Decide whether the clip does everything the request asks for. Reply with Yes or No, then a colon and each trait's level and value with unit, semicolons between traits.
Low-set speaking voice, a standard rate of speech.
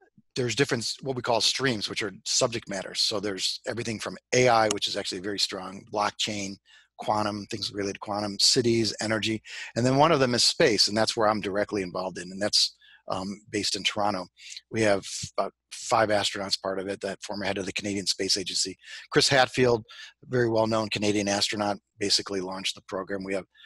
Yes: low, 105 Hz; average, 195 wpm